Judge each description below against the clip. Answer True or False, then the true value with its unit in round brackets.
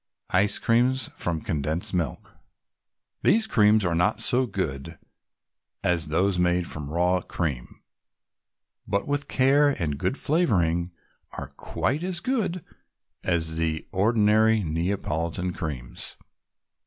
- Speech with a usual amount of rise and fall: False (6.6 semitones)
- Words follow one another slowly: True (115 wpm)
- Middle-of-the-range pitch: False (90 Hz)